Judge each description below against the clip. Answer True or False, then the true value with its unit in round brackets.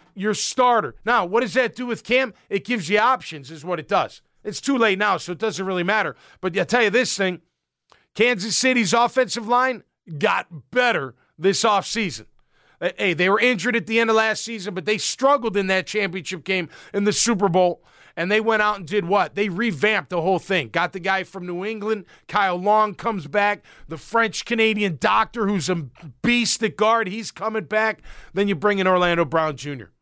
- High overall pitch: True (210 Hz)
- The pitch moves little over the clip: False (3.6 semitones)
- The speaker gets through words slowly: False (205 wpm)